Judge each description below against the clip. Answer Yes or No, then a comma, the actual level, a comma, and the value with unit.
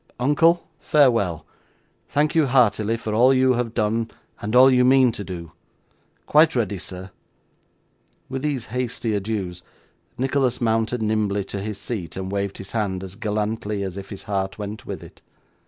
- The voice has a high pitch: No, low, 110 Hz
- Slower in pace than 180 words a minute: Yes, average, 160 wpm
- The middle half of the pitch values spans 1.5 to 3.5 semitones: No, average, 4.1 semitones